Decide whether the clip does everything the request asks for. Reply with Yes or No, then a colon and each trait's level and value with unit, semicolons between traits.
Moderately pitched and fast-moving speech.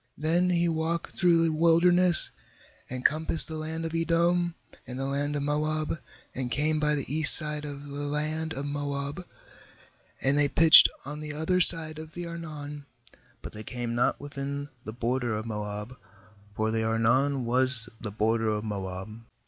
No: medium, 145 Hz; average, 170 wpm